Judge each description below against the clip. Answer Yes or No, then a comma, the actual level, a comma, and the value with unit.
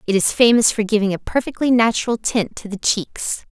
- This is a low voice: No, high, 220 Hz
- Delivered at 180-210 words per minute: Yes, fast, 205 wpm